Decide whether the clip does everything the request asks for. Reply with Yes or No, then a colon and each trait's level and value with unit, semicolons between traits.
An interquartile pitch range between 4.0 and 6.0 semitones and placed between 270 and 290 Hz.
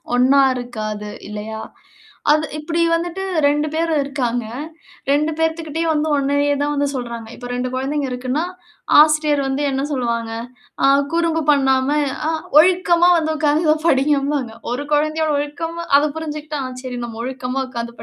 No: average, 3.5 semitones; very high, 285 Hz